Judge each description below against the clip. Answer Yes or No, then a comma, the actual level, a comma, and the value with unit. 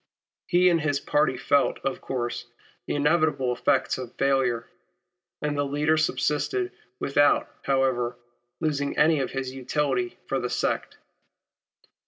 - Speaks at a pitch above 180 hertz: No, medium, 140 Hz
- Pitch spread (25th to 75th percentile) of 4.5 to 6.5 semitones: No, narrow, 2.5 semitones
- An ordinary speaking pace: No, slow, 130 wpm